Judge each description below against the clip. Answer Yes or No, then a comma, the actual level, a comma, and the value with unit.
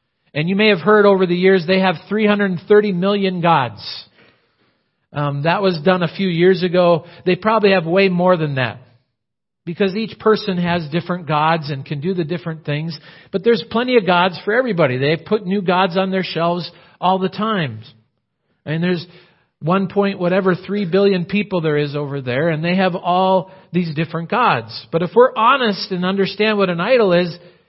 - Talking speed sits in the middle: Yes, average, 195 wpm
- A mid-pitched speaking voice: Yes, medium, 180 Hz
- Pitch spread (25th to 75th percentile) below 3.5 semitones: Yes, average, 2.9 semitones